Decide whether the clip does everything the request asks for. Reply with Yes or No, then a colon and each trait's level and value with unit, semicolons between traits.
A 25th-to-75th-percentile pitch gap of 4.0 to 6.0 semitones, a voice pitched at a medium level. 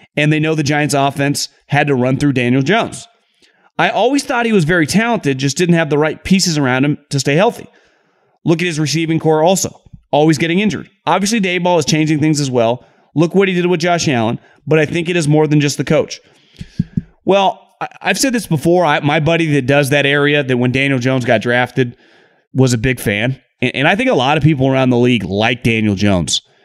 Yes: average, 4.6 semitones; medium, 150 Hz